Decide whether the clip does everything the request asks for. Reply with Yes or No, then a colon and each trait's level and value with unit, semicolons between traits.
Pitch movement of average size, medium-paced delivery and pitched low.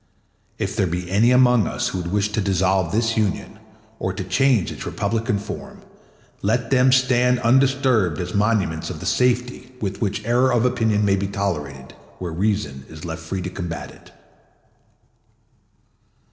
Yes: average, 5.0 semitones; average, 160 wpm; low, 105 Hz